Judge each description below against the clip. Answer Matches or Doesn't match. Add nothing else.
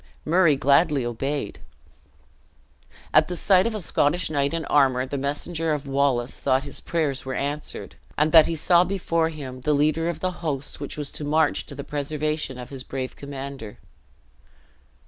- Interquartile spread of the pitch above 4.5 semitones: Doesn't match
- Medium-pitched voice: Matches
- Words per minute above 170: Doesn't match